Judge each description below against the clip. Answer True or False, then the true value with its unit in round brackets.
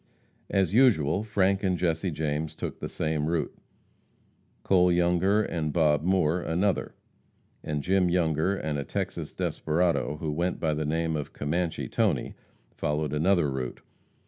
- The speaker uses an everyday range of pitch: True (3.2 semitones)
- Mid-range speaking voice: False (80 Hz)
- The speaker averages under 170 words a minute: True (145 wpm)